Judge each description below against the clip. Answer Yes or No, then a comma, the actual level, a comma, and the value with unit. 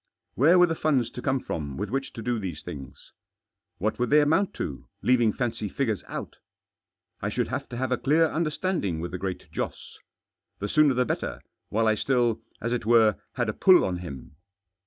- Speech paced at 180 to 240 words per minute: Yes, average, 200 wpm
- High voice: No, low, 120 Hz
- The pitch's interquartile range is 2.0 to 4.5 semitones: No, average, 5.3 semitones